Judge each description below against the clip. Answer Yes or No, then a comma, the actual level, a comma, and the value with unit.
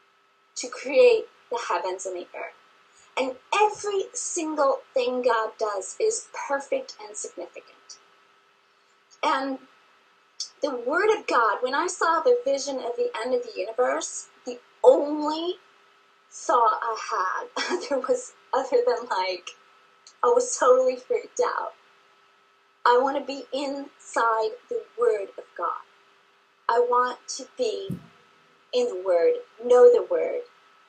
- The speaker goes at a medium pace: No, slow, 130 wpm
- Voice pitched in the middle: No, very high, 365 Hz